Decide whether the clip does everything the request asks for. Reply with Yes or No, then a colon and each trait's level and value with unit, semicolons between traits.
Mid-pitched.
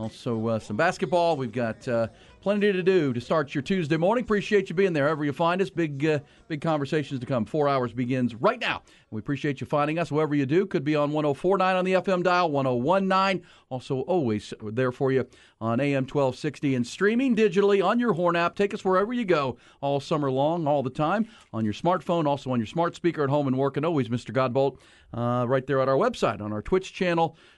Yes: medium, 150 Hz